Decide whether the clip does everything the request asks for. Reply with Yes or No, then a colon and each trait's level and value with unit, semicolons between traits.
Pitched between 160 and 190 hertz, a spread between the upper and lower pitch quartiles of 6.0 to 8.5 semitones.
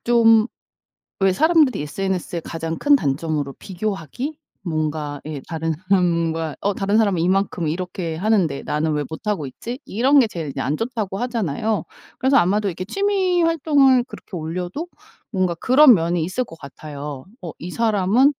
Yes: medium, 185 Hz; wide, 6.5 semitones